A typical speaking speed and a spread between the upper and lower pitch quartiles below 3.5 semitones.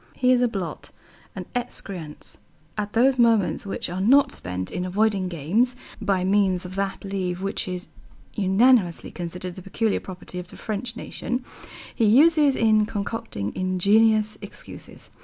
No: average, 150 wpm; average, 3.9 semitones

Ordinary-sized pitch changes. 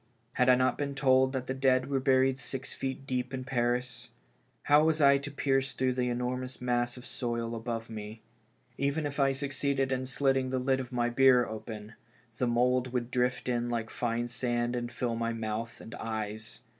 No: narrow, 1.9 semitones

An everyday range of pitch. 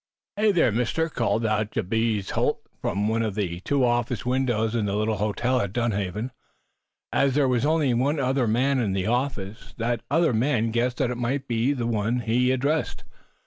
Yes: average, 3.3 semitones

